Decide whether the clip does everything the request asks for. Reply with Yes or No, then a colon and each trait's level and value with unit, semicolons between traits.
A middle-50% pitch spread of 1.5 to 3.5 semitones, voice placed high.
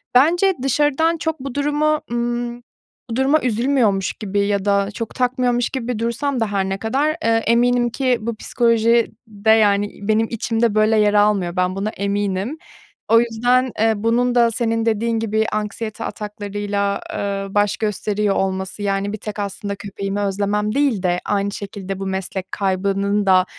Yes: average, 3.1 semitones; high, 215 Hz